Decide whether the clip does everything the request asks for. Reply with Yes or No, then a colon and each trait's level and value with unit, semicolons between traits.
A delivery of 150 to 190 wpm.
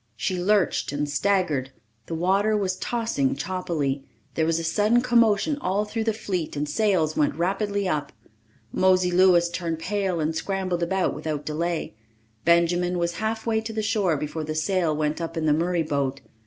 Yes: average, 170 wpm